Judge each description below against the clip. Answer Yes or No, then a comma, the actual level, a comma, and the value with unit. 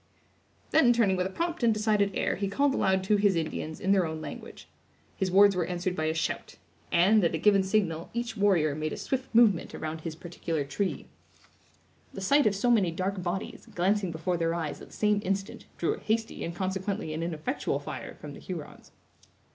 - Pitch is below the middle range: No, high, 190 Hz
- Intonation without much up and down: No, average, 3.8 semitones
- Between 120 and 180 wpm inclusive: No, fast, 205 wpm